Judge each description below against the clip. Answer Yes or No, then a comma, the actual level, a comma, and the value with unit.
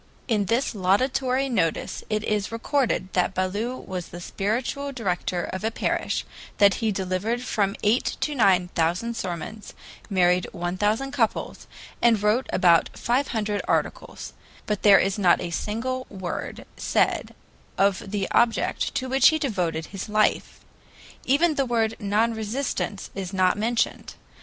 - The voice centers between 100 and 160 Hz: No, high, 210 Hz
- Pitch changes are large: No, average, 4.3 semitones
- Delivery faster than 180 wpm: No, average, 145 wpm